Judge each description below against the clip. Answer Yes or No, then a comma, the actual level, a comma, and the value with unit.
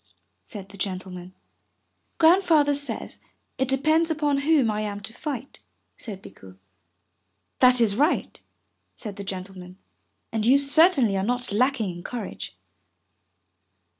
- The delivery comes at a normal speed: No, slow, 125 wpm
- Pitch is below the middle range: No, high, 235 Hz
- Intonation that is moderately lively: No, wide, 6.4 semitones